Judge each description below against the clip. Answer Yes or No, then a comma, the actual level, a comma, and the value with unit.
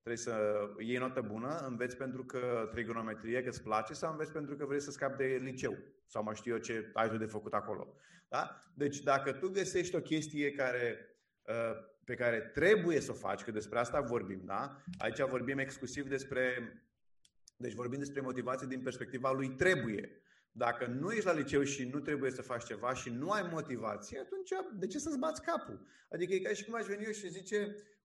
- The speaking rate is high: Yes, fast, 195 wpm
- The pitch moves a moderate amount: Yes, average, 4.2 semitones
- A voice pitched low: Yes, low, 130 Hz